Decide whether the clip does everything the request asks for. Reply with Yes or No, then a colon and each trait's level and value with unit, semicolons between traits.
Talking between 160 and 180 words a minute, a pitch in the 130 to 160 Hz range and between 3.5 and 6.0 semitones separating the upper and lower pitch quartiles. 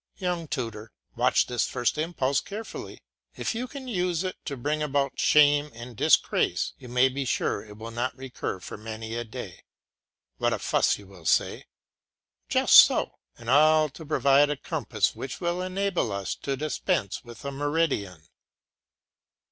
Yes: average, 165 wpm; medium, 140 Hz; average, 5.1 semitones